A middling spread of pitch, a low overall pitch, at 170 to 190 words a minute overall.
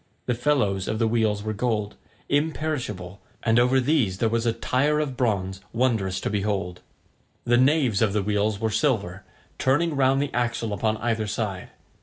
Yes: average, 4.0 semitones; low, 115 Hz; average, 175 wpm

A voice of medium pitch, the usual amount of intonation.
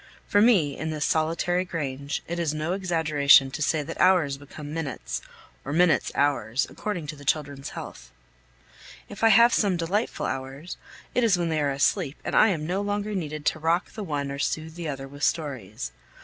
Yes: medium, 155 Hz; average, 4.1 semitones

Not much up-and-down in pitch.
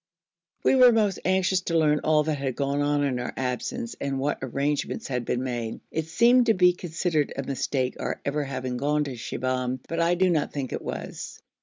No: average, 5.0 semitones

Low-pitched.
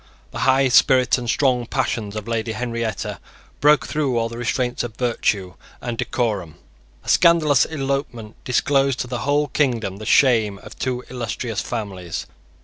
Yes: low, 120 Hz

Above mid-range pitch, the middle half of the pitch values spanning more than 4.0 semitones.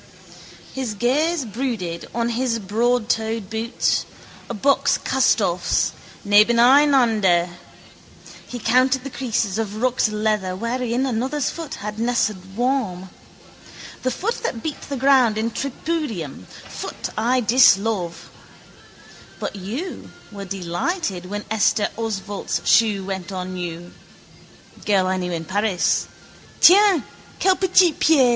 Yes: high, 225 Hz; average, 4.8 semitones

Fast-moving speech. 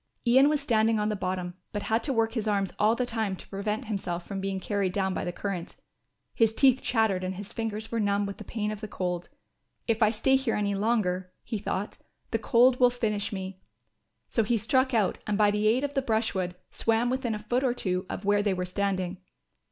Yes: fast, 225 wpm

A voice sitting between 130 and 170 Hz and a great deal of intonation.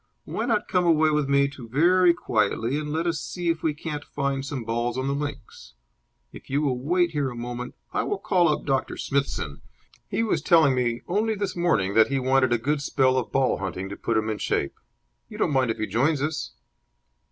No: medium, 140 Hz; average, 5.0 semitones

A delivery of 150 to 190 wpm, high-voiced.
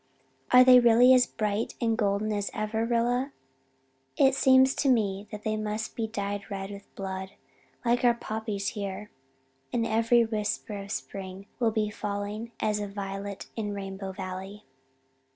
Yes: average, 155 wpm; high, 210 Hz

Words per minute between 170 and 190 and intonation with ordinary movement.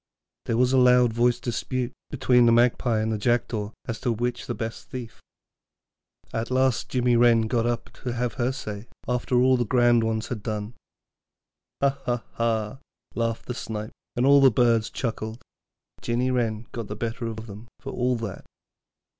No: average, 185 wpm; narrow, 1.7 semitones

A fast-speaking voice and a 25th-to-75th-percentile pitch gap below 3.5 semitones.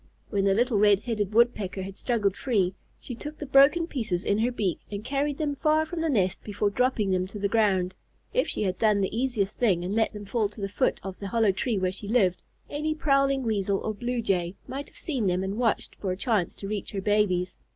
No: fast, 235 wpm; average, 4.4 semitones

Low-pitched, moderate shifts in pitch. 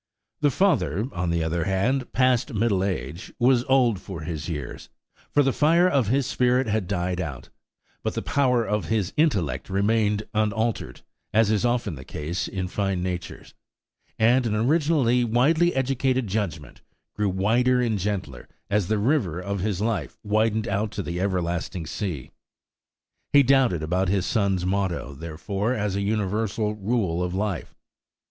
Yes: low, 105 Hz; average, 5.0 semitones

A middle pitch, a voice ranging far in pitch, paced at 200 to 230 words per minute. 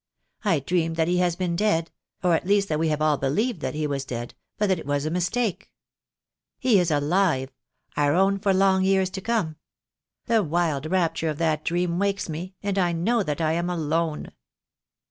No: medium, 170 Hz; average, 3.7 semitones; fast, 205 wpm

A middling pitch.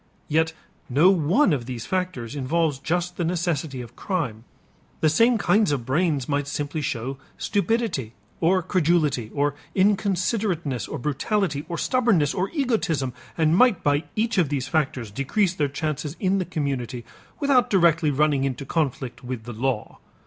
Yes: medium, 155 Hz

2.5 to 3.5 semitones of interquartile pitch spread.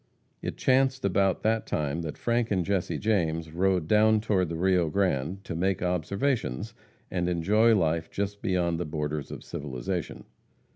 No: average, 4.2 semitones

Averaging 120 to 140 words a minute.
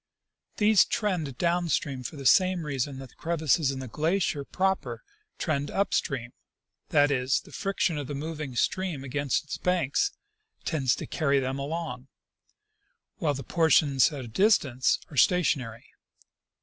No: average, 155 wpm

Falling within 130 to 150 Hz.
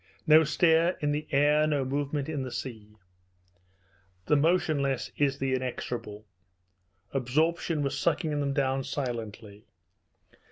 Yes: medium, 140 Hz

